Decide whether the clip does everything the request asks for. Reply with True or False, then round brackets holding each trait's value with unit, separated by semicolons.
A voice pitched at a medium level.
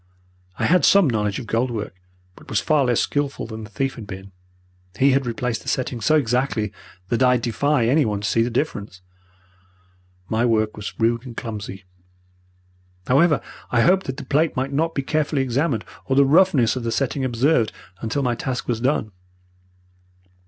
False (125 Hz)